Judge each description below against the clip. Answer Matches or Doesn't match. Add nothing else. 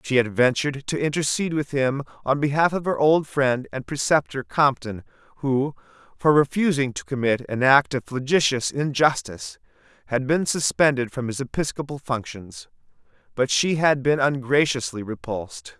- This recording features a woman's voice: Doesn't match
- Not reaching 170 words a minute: Matches